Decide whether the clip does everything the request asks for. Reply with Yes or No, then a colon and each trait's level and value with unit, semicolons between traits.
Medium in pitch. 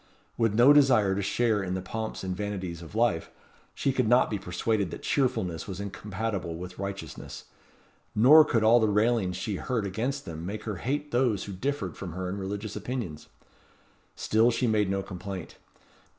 No: low, 105 Hz